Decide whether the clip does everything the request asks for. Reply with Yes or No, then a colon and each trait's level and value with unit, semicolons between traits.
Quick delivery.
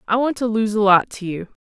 Yes: fast, 295 wpm